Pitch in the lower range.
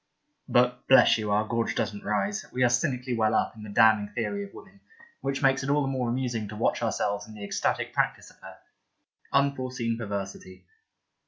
Yes: low, 120 Hz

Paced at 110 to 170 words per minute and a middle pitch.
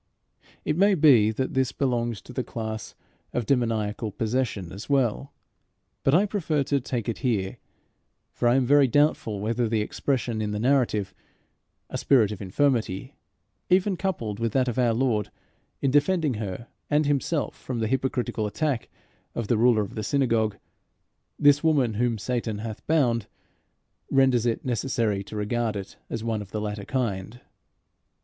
No: average, 160 wpm; low, 120 Hz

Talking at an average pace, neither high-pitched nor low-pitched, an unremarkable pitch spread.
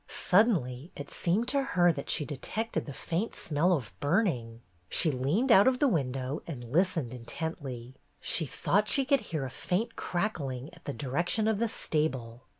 No: average, 170 wpm; medium, 160 Hz; wide, 7.7 semitones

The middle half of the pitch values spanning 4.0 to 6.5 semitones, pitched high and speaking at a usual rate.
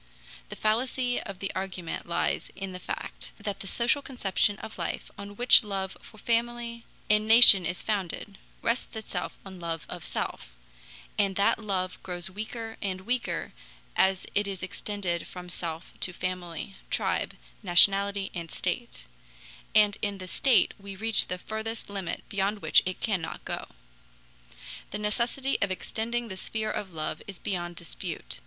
No: average, 3.1 semitones; high, 200 Hz; average, 155 wpm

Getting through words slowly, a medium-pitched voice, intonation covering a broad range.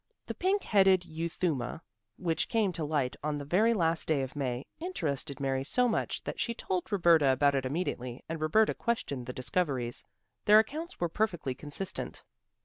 No: average, 170 wpm; medium, 160 Hz; wide, 6.1 semitones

